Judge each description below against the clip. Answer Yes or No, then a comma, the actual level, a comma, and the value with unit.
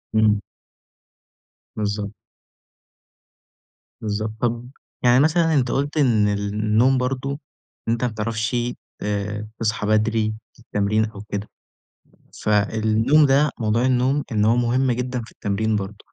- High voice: No, low, 110 Hz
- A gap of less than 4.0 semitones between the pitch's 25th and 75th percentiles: Yes, average, 3.1 semitones